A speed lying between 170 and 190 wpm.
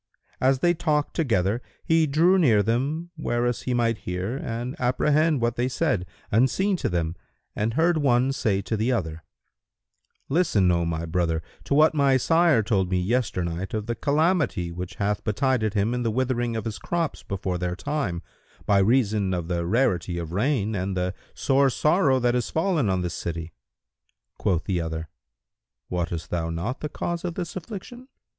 Yes: average, 175 wpm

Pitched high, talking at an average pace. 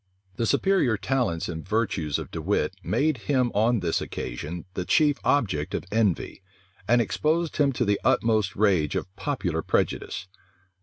No: low, 110 Hz; average, 155 wpm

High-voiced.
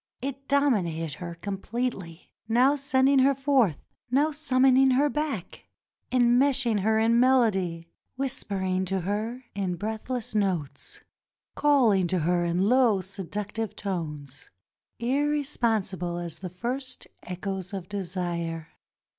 Yes: high, 215 Hz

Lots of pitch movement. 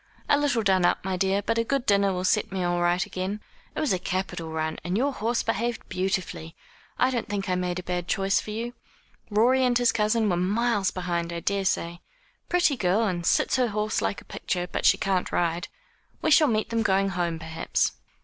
No: average, 4.2 semitones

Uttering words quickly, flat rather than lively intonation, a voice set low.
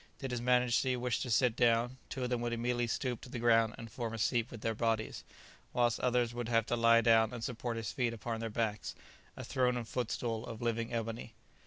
Yes: fast, 225 wpm; narrow, 1.3 semitones; low, 115 Hz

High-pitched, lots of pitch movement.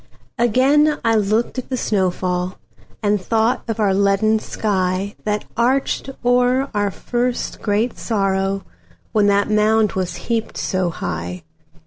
No: high, 210 Hz; average, 3.5 semitones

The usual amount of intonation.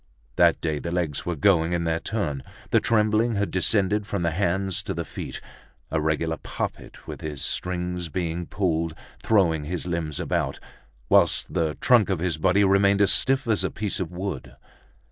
Yes: average, 3.5 semitones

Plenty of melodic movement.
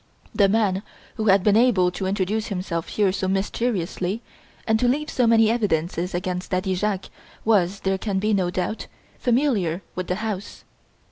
No: average, 3.2 semitones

